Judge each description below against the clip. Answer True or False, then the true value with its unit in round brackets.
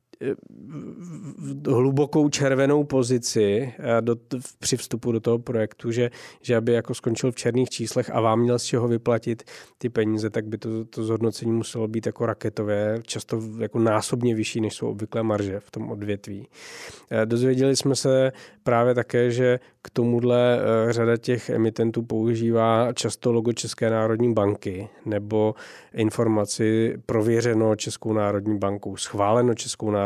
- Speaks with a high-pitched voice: False (115 Hz)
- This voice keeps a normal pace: True (150 wpm)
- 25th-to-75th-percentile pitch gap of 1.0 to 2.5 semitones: True (1.7 semitones)